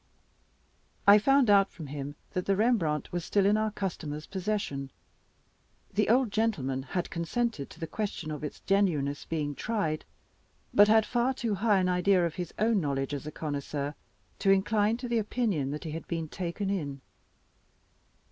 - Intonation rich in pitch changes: Yes, wide, 5.9 semitones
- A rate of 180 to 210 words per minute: No, average, 170 wpm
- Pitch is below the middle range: No, medium, 185 Hz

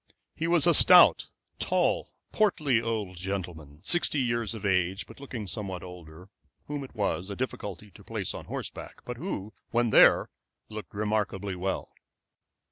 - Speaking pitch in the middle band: No, low, 105 Hz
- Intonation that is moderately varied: Yes, average, 4.8 semitones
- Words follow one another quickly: No, average, 150 wpm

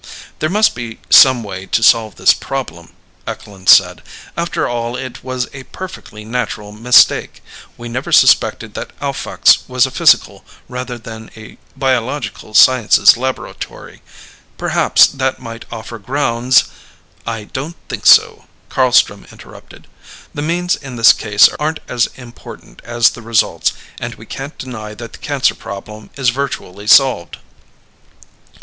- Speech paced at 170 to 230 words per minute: No, average, 140 wpm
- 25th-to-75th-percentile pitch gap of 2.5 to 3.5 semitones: Yes, average, 2.9 semitones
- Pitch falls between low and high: No, low, 120 Hz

